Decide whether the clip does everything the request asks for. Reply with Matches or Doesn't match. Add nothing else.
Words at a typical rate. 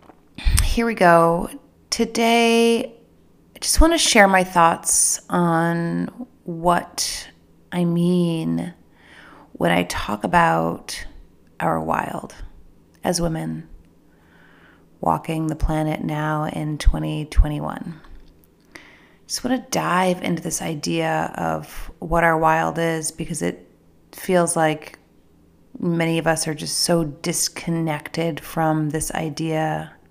Doesn't match